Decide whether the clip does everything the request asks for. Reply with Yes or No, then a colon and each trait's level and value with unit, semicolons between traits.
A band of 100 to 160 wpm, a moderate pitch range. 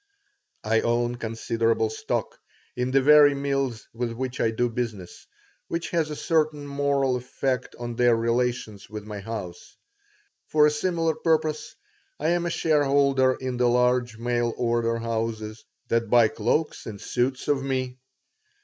Yes: average, 150 wpm; average, 3.5 semitones